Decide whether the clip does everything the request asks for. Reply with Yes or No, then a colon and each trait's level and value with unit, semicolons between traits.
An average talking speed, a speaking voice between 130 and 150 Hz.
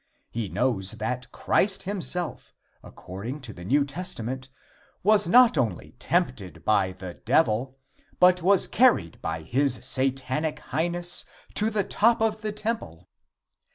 No: slow, 130 wpm; low, 135 Hz